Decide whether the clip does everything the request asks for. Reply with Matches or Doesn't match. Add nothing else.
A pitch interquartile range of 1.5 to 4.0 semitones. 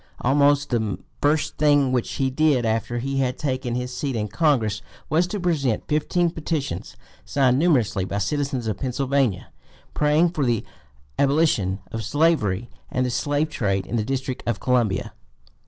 Doesn't match